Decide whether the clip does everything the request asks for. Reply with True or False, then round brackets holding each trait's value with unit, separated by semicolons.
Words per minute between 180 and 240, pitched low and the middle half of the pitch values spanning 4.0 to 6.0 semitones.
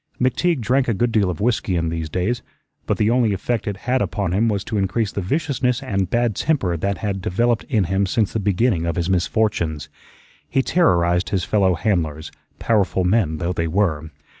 True (195 wpm; 100 Hz; 4.7 semitones)